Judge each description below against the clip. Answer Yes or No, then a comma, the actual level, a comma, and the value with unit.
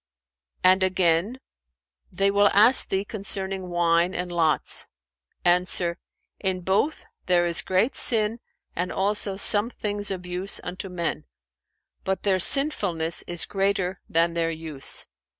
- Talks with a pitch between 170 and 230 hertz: Yes, medium, 185 Hz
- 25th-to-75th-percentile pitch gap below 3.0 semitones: Yes, narrow, 2.5 semitones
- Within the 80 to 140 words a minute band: Yes, slow, 135 wpm